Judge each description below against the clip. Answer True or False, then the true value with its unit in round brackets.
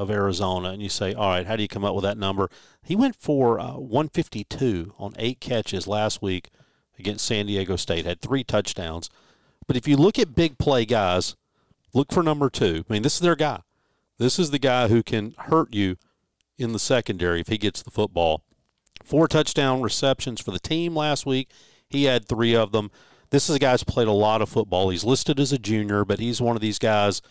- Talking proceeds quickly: True (220 wpm)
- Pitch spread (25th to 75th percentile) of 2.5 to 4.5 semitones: False (5.3 semitones)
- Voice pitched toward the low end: True (110 Hz)